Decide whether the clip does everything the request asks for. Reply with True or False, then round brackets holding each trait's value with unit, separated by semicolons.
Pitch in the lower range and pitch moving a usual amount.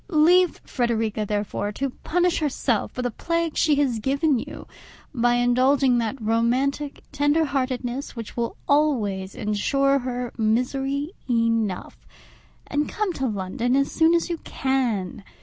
False (255 Hz; 4.0 semitones)